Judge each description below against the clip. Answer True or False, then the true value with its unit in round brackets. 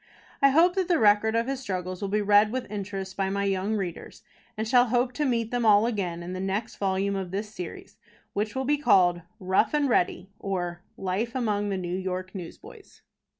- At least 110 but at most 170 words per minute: False (205 wpm)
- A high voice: True (205 Hz)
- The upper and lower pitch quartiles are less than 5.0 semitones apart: True (3.7 semitones)